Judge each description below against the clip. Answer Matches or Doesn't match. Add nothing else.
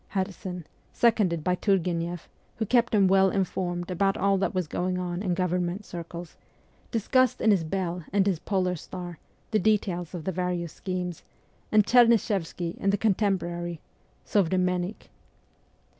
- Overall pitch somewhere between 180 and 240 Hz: Matches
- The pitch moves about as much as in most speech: Doesn't match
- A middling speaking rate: Matches